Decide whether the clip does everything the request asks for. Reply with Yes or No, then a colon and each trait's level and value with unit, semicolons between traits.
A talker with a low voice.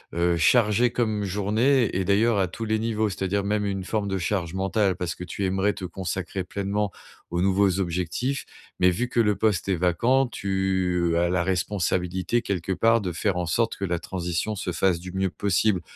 Yes: very low, 95 Hz